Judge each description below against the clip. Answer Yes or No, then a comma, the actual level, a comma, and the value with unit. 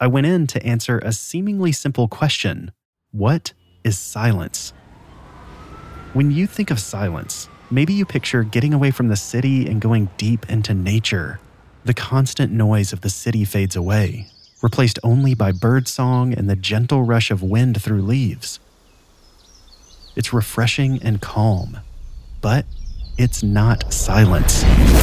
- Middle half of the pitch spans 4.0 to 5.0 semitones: Yes, average, 4.4 semitones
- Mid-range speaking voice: No, low, 110 Hz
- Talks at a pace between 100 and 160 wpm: Yes, average, 140 wpm